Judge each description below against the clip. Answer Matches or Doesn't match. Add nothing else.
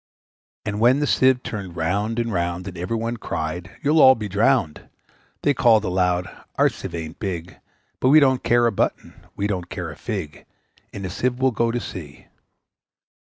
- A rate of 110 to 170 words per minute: Doesn't match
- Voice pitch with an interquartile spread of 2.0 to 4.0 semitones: Doesn't match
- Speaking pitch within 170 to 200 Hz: Doesn't match